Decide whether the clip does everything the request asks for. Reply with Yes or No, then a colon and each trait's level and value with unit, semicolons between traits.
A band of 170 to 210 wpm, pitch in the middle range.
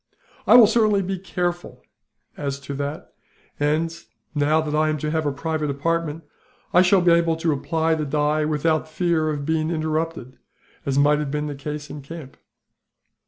Yes: average, 180 wpm; medium, 155 Hz